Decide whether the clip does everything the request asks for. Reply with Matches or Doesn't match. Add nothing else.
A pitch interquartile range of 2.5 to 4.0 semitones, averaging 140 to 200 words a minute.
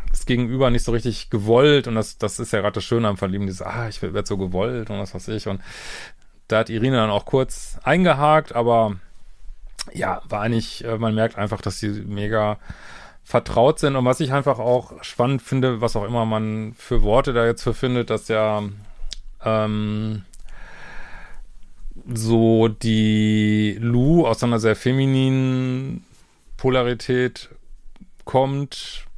Matches